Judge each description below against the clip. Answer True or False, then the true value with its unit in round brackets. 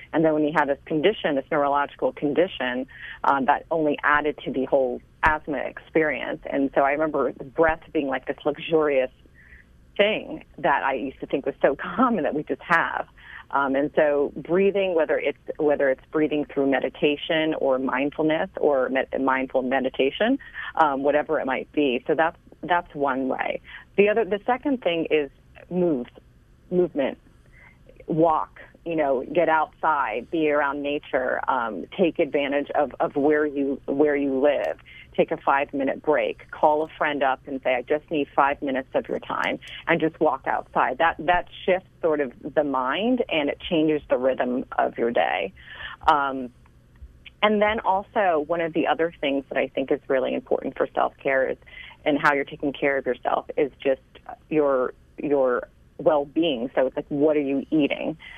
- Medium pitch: True (150 Hz)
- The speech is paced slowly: False (175 wpm)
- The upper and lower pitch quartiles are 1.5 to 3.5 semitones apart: True (2.9 semitones)